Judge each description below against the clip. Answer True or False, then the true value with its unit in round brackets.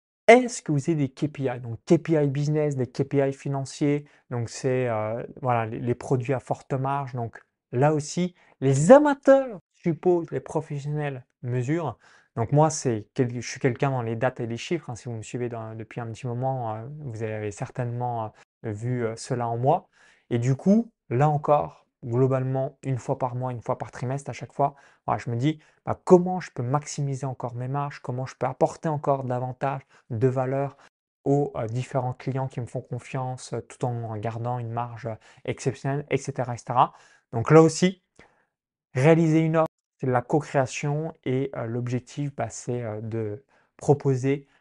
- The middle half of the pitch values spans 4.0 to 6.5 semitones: False (3.3 semitones)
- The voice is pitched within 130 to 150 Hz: True (135 Hz)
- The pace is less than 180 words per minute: True (170 wpm)